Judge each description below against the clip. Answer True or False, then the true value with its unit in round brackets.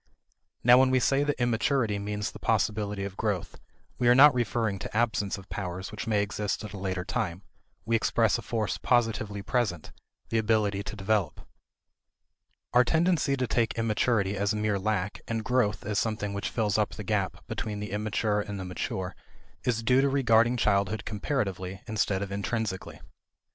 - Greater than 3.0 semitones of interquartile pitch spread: False (2.7 semitones)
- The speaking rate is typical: True (175 wpm)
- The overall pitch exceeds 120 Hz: False (105 Hz)